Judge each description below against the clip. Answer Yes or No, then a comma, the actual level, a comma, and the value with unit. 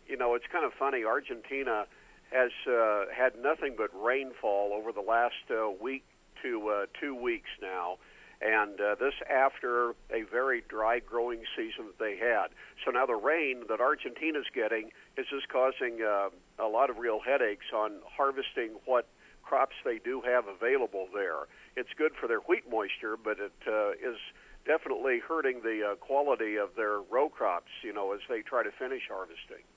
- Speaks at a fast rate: No, average, 175 wpm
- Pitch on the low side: Yes, low, 130 Hz